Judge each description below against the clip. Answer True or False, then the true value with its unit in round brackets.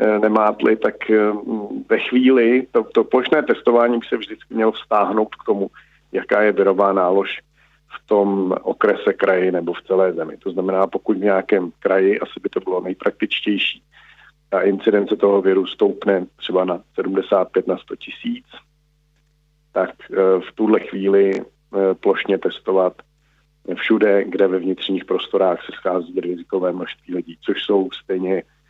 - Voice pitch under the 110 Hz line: True (100 Hz)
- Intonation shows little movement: False (3.1 semitones)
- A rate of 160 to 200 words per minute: False (140 wpm)